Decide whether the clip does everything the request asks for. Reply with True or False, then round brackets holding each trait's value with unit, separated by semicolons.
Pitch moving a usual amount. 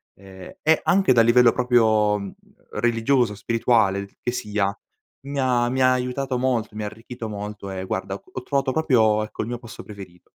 True (3.4 semitones)